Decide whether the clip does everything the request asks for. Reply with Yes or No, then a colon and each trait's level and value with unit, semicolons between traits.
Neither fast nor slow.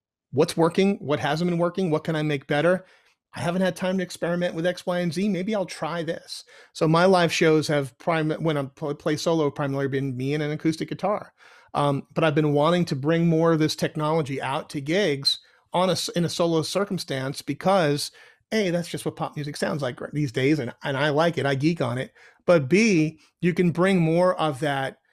No: fast, 215 wpm